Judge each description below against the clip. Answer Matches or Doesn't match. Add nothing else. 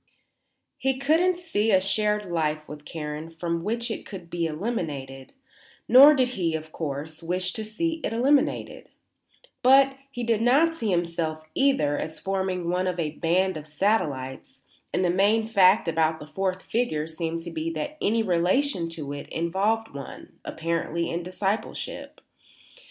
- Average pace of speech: Matches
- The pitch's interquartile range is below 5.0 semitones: Doesn't match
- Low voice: Doesn't match